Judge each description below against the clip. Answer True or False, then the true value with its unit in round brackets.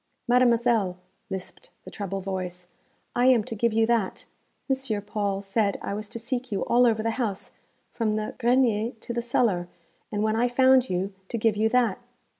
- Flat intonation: False (3.2 semitones)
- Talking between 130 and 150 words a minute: False (185 wpm)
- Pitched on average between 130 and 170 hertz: False (220 Hz)